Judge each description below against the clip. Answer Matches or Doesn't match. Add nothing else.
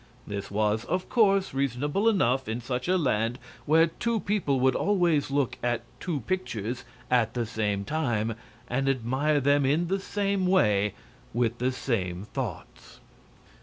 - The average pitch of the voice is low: Matches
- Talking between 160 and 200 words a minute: Doesn't match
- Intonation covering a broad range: Matches